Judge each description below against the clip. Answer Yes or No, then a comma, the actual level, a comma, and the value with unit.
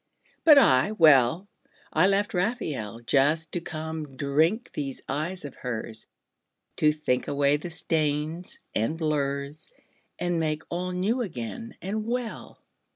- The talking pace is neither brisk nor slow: No, slow, 130 wpm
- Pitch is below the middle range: No, medium, 155 Hz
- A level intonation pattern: No, average, 4.6 semitones